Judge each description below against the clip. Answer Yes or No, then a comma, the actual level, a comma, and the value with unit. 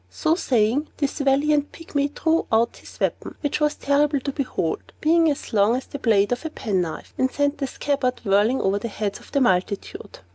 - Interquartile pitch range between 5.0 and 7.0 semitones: Yes, average, 5.3 semitones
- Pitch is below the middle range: No, very high, 270 Hz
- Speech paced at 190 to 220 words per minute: Yes, average, 195 wpm